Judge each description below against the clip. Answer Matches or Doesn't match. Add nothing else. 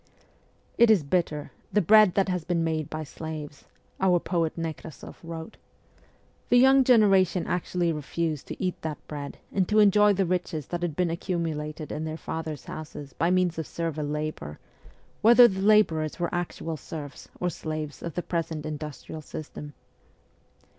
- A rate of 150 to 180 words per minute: Matches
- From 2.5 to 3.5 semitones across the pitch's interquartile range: Matches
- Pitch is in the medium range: Matches